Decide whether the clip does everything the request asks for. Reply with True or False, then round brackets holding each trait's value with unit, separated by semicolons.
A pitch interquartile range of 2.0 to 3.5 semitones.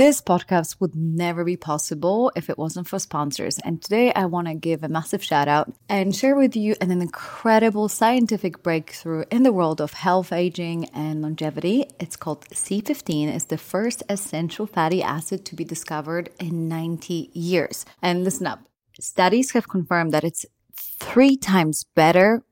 False (3.9 semitones)